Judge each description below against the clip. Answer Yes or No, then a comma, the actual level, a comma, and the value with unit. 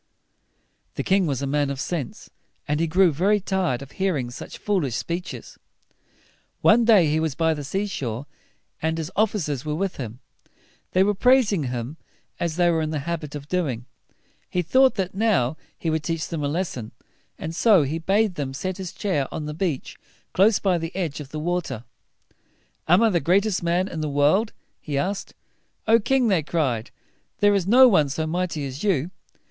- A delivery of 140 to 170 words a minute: No, average, 195 wpm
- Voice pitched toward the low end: No, medium, 165 Hz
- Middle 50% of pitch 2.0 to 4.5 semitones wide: No, average, 4.9 semitones